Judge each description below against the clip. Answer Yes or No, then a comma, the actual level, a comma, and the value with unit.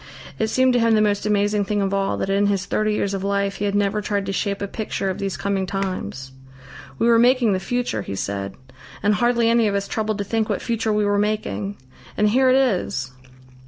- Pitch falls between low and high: No, high, 205 Hz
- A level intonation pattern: Yes, narrow, 2.0 semitones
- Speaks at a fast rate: Yes, fast, 235 wpm